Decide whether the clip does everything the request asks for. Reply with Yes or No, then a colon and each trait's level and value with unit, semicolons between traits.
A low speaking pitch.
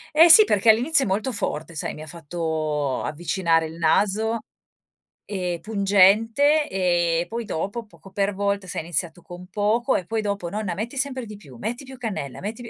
No: high, 200 Hz